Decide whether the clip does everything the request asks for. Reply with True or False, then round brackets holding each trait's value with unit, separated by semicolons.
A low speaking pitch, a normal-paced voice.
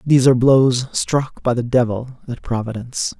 True (125 Hz; 170 wpm)